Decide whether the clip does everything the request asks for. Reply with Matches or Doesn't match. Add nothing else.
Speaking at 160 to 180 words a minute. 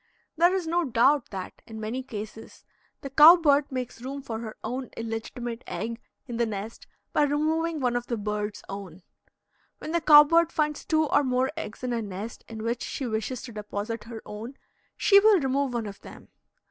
Doesn't match